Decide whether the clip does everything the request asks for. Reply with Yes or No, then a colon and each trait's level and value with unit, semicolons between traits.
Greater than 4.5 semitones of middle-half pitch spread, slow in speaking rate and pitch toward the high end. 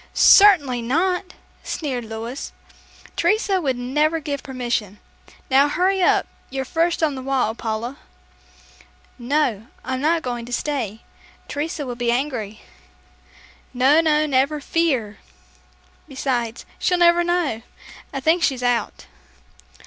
Yes: average, 4.9 semitones; slow, 120 wpm; very high, 270 Hz